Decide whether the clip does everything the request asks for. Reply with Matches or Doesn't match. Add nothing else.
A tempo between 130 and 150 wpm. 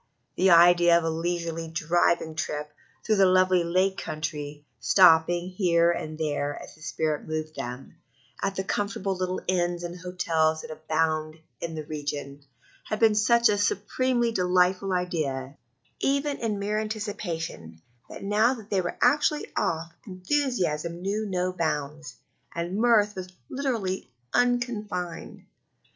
Matches